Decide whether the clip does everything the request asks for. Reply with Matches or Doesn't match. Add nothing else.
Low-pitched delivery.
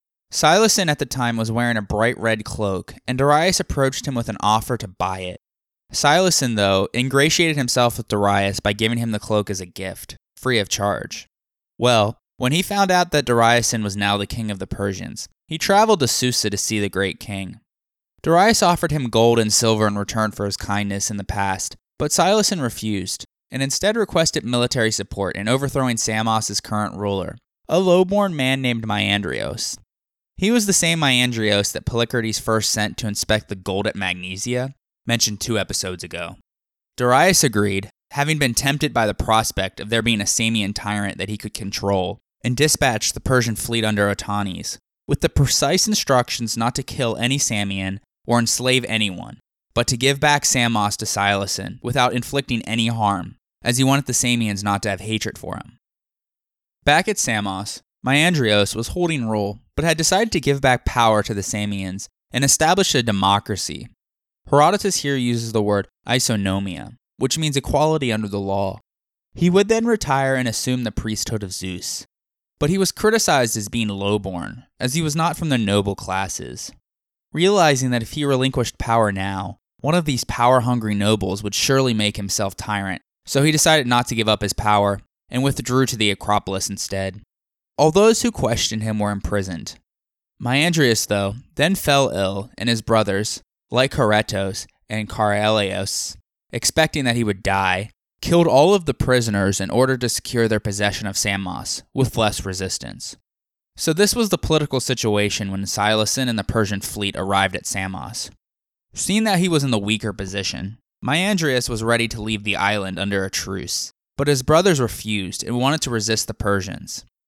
Matches